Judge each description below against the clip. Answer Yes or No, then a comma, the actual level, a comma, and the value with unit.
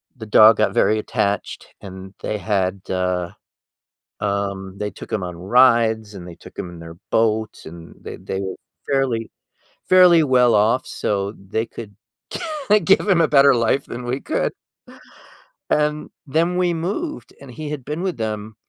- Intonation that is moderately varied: No, wide, 5.9 semitones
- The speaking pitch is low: Yes, low, 110 Hz